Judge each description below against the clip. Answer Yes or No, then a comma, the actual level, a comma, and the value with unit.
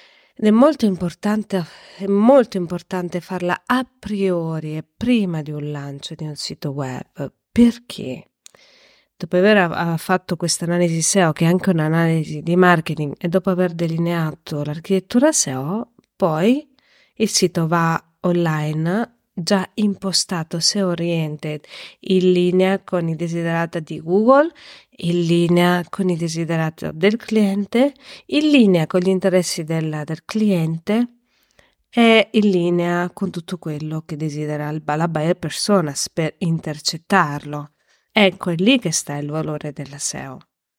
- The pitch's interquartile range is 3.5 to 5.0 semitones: Yes, average, 3.9 semitones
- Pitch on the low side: No, medium, 175 Hz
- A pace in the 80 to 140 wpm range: Yes, average, 135 wpm